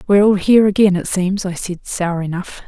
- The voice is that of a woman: Yes, female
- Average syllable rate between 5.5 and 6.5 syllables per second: Yes, 5.7 syllables/s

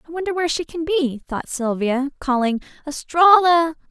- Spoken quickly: No, average, 155 wpm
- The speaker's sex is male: No, female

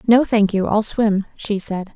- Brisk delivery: Yes, fast, 215 wpm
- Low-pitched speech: No, high, 210 Hz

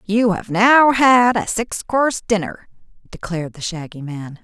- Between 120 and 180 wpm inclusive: Yes, average, 160 wpm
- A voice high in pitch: Yes, high, 205 Hz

